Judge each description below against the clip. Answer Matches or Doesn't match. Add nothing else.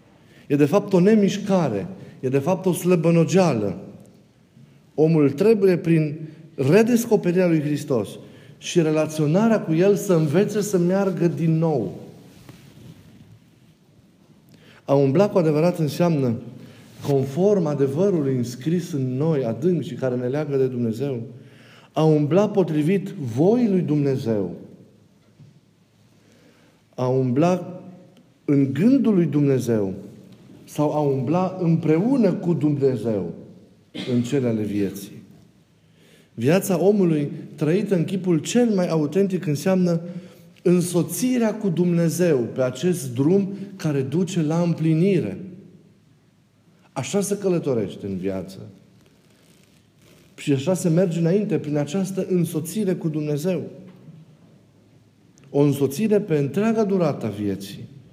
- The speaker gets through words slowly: Matches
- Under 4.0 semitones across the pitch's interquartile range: Doesn't match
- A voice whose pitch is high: Doesn't match